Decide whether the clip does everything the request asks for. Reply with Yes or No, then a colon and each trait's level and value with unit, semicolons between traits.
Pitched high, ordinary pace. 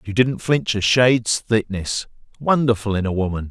No: low, 110 Hz; average, 170 wpm